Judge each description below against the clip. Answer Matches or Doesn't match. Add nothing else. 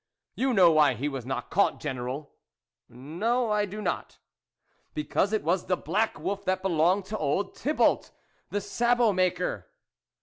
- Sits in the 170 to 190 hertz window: Matches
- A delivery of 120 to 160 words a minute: Doesn't match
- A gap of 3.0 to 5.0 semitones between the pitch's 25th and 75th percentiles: Doesn't match